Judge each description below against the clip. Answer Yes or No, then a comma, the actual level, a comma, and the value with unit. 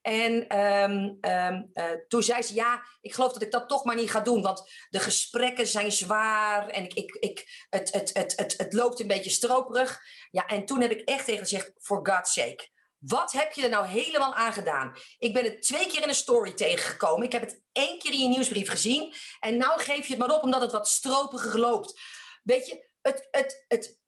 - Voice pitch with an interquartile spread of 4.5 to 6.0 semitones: Yes, average, 4.8 semitones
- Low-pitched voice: No, high, 240 Hz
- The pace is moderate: No, fast, 230 wpm